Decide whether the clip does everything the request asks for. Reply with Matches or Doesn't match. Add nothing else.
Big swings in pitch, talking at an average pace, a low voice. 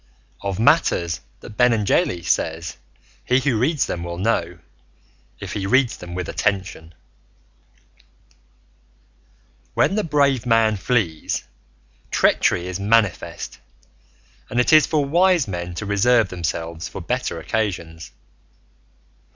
Doesn't match